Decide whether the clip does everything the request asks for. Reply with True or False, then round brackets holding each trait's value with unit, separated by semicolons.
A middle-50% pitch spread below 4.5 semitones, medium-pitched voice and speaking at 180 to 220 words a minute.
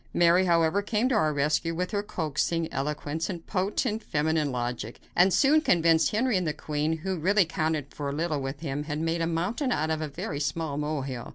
True (3.6 semitones; 160 Hz; 205 wpm)